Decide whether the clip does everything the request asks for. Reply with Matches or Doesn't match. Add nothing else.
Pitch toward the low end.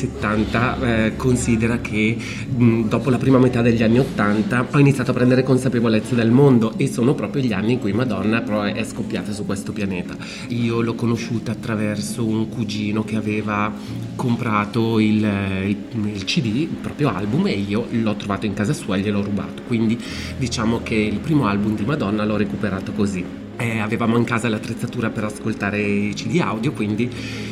Matches